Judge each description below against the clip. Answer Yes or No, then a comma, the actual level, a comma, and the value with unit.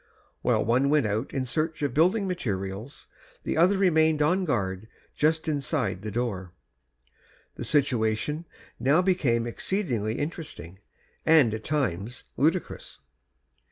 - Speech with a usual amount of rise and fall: No, wide, 6.4 semitones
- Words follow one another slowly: Yes, slow, 120 wpm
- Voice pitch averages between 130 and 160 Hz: Yes, medium, 140 Hz